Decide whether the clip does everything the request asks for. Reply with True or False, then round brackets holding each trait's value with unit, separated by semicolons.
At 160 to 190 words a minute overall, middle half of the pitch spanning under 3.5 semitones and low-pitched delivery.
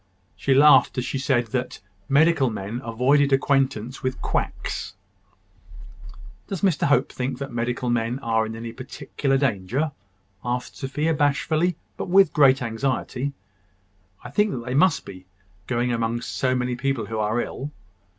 False (145 wpm; 3.0 semitones; 130 Hz)